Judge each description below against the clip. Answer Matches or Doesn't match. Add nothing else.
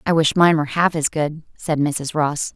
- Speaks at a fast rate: Matches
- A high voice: Doesn't match